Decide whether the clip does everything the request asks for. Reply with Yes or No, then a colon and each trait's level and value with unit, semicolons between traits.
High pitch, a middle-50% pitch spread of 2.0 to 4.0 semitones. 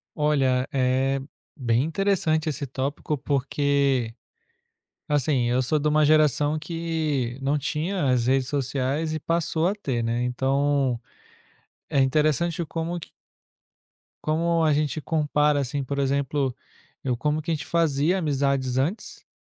No: medium, 145 Hz; average, 2.9 semitones